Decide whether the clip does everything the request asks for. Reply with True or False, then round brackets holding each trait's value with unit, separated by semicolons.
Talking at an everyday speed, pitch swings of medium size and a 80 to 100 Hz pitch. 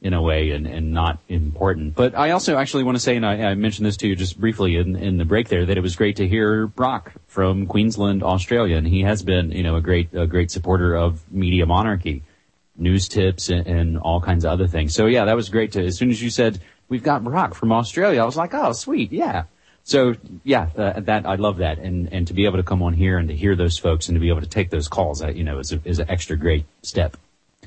False (265 wpm; 3.8 semitones; 95 Hz)